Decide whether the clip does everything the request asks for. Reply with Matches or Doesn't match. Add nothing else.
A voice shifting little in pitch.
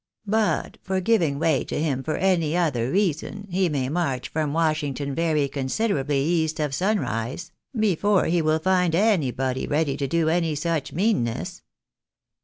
Doesn't match